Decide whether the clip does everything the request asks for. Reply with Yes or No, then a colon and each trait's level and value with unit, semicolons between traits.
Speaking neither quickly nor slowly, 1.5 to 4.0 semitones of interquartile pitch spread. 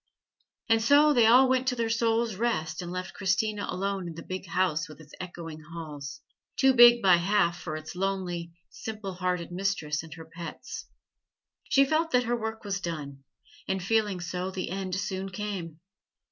No: average, 175 wpm; average, 4.7 semitones